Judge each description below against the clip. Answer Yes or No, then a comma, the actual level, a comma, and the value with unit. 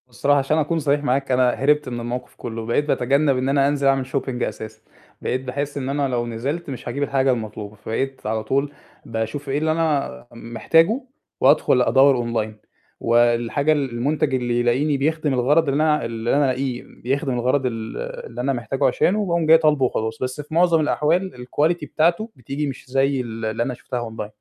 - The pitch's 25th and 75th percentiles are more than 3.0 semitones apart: Yes, average, 3.4 semitones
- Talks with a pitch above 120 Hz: Yes, low, 135 Hz